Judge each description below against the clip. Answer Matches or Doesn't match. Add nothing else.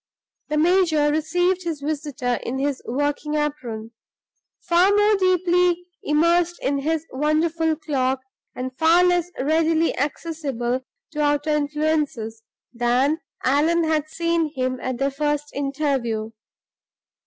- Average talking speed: Doesn't match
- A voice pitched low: Doesn't match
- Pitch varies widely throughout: Doesn't match